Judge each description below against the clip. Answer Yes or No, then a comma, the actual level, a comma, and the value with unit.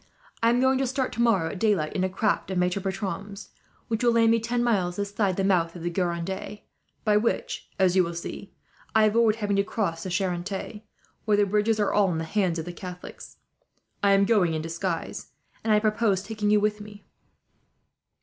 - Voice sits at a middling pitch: No, high, 200 Hz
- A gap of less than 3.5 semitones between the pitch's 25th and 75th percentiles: Yes, average, 3.0 semitones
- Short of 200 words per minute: No, fast, 205 wpm